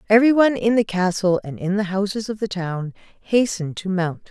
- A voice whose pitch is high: Yes, high, 200 Hz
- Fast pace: Yes, fast, 210 wpm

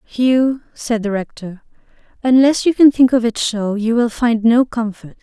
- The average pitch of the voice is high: Yes, high, 235 Hz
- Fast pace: No, average, 185 wpm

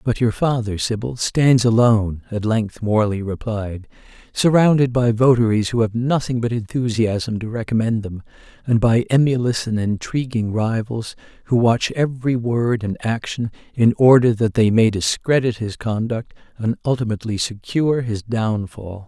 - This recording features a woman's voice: No, male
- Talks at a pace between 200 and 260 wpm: No, average, 145 wpm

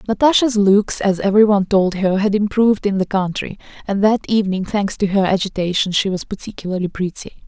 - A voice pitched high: Yes, high, 200 Hz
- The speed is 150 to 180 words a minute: Yes, average, 175 wpm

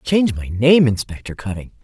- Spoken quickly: No, average, 165 wpm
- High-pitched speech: No, low, 120 Hz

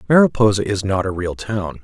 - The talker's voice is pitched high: No, low, 100 Hz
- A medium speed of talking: Yes, average, 195 wpm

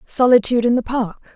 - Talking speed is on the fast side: No, average, 175 wpm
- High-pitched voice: Yes, high, 235 Hz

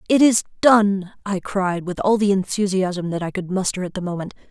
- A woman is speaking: Yes, female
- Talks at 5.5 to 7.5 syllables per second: No, 5.2 syllables/s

